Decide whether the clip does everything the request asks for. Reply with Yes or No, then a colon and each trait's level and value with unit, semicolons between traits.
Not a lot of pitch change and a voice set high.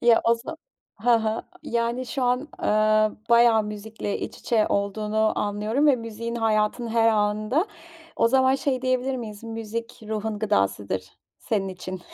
Yes: narrow, 2.1 semitones; high, 225 Hz